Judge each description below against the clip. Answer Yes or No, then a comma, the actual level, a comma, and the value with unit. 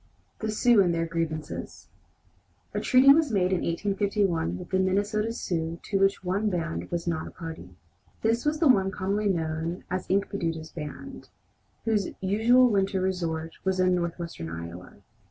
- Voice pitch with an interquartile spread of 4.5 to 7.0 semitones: No, average, 3.9 semitones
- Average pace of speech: Yes, average, 155 wpm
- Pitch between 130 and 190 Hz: Yes, medium, 185 Hz